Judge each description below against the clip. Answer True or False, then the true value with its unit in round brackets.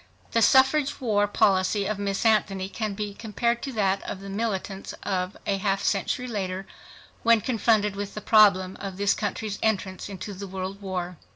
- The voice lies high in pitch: True (200 Hz)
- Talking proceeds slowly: False (170 wpm)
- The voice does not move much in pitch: True (2.1 semitones)